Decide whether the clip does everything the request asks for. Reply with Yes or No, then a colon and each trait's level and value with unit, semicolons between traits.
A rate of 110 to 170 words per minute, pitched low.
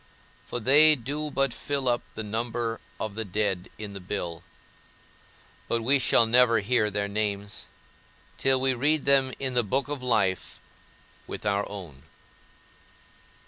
Yes: average, 145 wpm; low, 115 Hz